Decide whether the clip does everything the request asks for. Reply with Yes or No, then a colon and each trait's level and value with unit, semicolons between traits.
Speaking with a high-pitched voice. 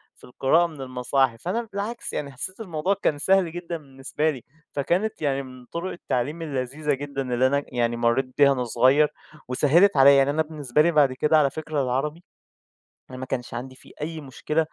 No: medium, 140 Hz